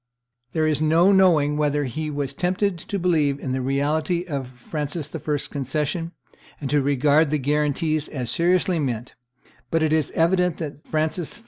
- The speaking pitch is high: No, medium, 150 Hz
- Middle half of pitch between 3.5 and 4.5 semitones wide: No, average, 2.7 semitones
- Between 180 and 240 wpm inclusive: No, average, 165 wpm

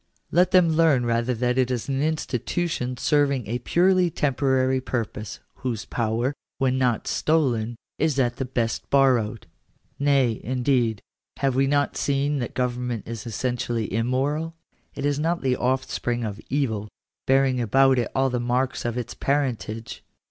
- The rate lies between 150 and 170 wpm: Yes, average, 155 wpm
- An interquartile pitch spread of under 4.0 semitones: Yes, average, 2.7 semitones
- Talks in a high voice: No, low, 130 Hz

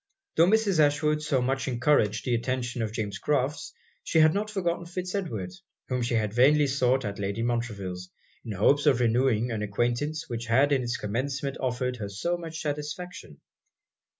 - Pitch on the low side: Yes, low, 130 Hz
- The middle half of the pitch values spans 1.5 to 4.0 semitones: No, average, 4.6 semitones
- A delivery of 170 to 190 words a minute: Yes, average, 175 wpm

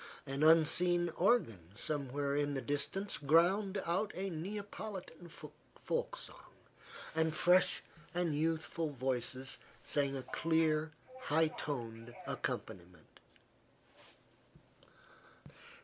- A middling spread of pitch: Yes, average, 3.9 semitones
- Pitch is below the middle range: No, medium, 155 Hz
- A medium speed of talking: No, slow, 90 wpm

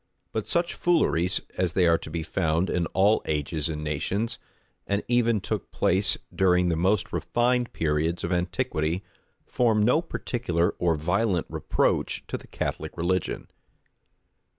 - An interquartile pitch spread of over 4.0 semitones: Yes, average, 4.4 semitones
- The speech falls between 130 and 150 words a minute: Yes, average, 145 wpm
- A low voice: Yes, very low, 90 Hz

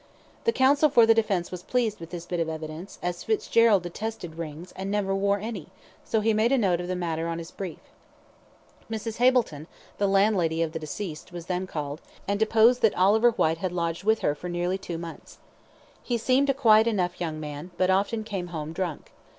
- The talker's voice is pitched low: No, medium, 185 Hz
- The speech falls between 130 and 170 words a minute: No, fast, 205 wpm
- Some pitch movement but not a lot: Yes, average, 4.7 semitones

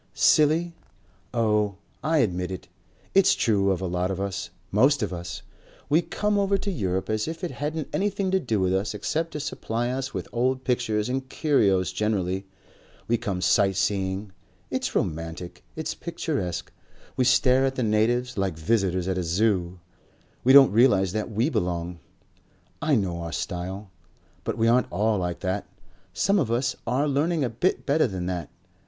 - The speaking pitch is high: No, low, 110 Hz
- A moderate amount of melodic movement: No, wide, 6.4 semitones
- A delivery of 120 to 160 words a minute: No, average, 170 wpm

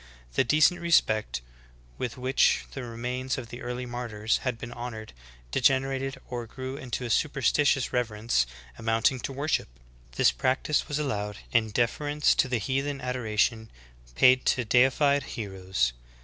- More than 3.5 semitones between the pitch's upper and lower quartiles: No, average, 3.1 semitones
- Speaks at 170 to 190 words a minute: No, average, 140 wpm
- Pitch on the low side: Yes, low, 125 Hz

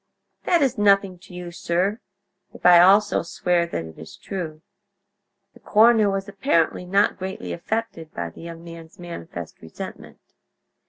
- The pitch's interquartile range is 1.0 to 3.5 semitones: Yes, average, 3.2 semitones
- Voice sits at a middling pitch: Yes, medium, 180 Hz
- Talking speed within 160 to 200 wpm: No, average, 150 wpm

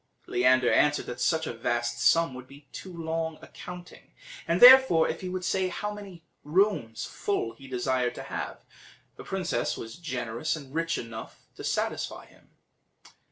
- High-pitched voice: No, medium, 155 Hz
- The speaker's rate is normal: Yes, average, 165 wpm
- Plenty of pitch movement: Yes, wide, 6.3 semitones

